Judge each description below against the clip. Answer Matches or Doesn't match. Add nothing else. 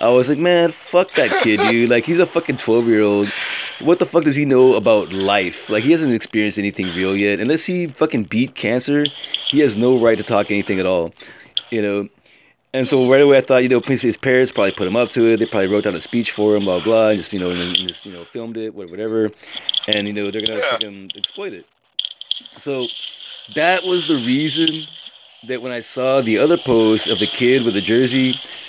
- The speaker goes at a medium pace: Doesn't match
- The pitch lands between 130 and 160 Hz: Doesn't match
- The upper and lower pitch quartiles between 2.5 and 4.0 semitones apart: Doesn't match